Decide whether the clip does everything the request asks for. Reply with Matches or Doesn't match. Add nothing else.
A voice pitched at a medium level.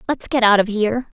Doesn't match